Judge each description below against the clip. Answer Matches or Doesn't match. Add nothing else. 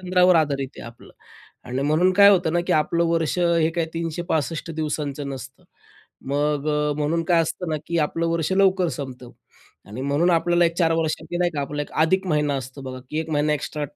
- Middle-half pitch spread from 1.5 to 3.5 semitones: Matches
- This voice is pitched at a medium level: Matches